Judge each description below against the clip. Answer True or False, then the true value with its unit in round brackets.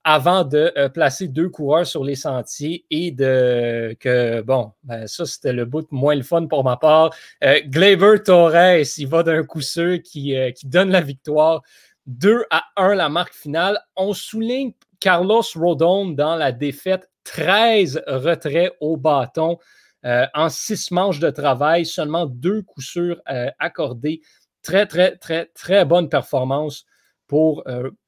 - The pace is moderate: True (160 wpm)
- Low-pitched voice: False (160 Hz)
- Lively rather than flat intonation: False (4.3 semitones)